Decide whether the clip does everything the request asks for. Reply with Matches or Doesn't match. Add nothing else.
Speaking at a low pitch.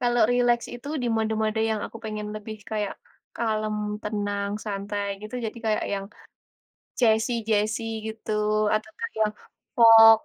Doesn't match